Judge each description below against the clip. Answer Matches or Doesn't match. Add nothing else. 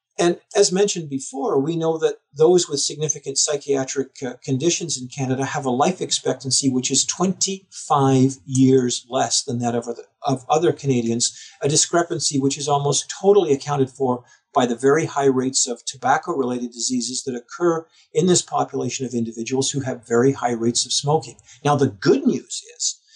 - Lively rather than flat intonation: Doesn't match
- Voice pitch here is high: Doesn't match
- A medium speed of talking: Matches